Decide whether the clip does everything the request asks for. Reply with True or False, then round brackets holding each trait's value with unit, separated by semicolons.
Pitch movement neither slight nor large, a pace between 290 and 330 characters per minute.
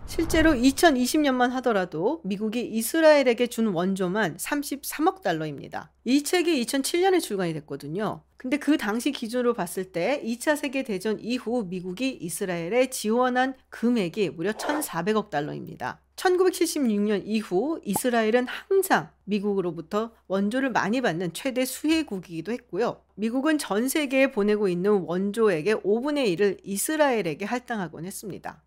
False (5.8 semitones; 310 characters per minute)